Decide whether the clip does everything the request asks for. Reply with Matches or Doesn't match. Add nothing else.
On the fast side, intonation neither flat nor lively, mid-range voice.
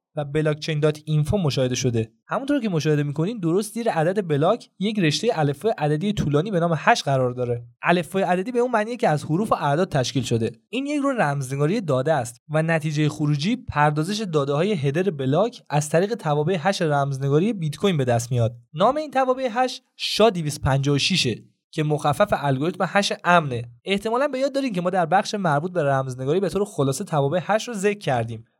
Doesn't match